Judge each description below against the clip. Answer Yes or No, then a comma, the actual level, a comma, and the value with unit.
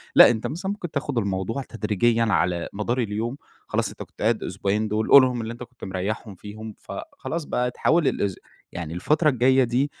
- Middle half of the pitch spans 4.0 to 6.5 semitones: Yes, average, 4.3 semitones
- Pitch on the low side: Yes, low, 115 Hz